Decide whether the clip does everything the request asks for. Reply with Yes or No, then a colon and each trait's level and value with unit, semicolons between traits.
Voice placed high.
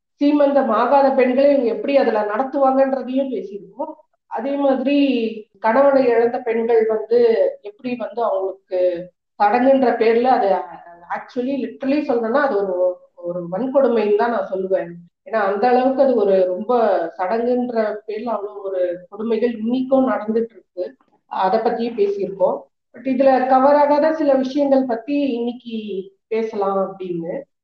Yes: high, 235 Hz